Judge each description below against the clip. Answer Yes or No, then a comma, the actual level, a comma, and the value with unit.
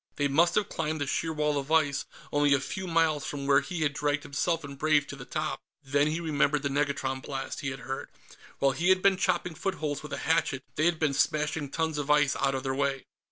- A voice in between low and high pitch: Yes, medium, 145 Hz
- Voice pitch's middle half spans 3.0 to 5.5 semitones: No, narrow, 2.4 semitones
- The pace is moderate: No, fast, 240 wpm